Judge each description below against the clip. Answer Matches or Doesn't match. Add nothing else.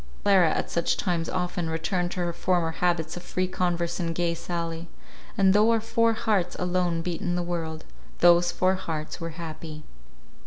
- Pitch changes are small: Matches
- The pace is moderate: Matches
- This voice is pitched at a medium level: Matches